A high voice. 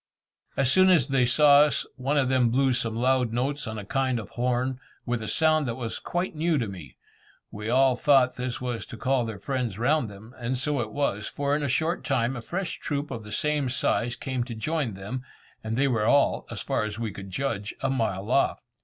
No: low, 125 Hz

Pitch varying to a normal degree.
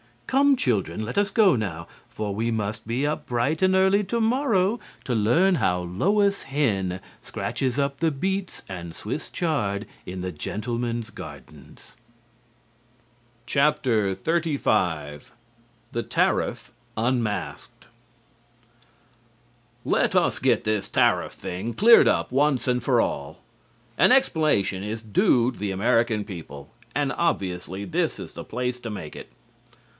No: wide, 7.7 semitones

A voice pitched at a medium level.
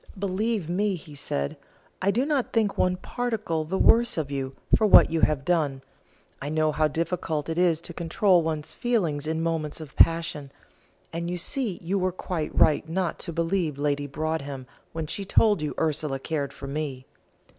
Yes: medium, 165 Hz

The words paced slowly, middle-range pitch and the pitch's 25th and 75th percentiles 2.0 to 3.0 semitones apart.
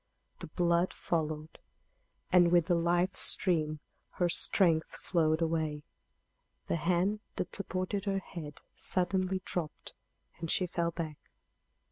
Yes: slow, 120 wpm; medium, 170 Hz; narrow, 2.5 semitones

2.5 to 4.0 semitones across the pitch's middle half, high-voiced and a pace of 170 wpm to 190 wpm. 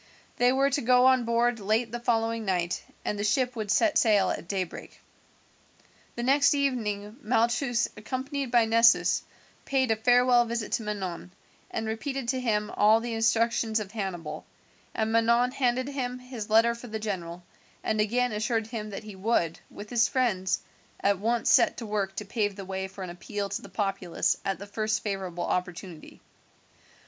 Yes: average, 3.3 semitones; high, 220 Hz; average, 175 wpm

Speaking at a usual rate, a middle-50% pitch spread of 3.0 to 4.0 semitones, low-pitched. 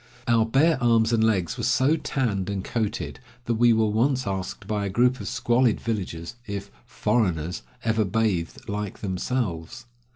Yes: average, 160 wpm; average, 3.5 semitones; low, 110 Hz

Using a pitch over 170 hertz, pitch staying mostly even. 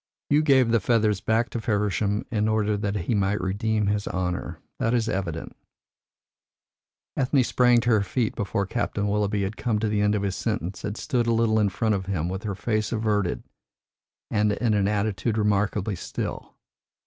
No: low, 105 Hz; narrow, 2.1 semitones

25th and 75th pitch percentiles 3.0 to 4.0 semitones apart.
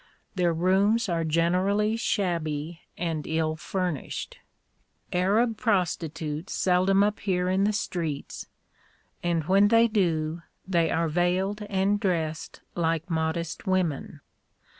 Yes: average, 3.3 semitones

